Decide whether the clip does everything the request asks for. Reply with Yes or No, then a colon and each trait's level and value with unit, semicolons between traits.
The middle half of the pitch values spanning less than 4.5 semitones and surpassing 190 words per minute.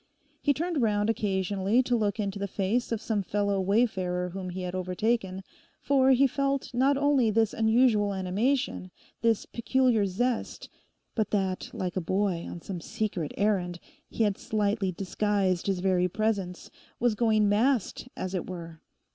No: average, 3.8 semitones; average, 155 wpm